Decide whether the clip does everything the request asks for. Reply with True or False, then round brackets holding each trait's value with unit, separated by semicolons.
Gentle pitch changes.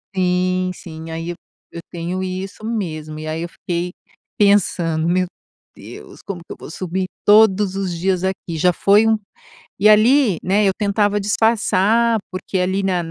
False (3.0 semitones)